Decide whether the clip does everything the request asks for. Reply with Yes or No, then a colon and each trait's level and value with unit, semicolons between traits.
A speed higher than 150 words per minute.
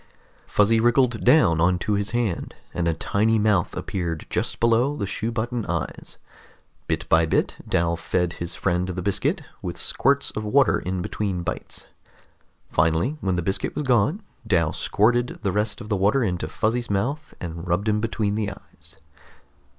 Yes: average, 165 wpm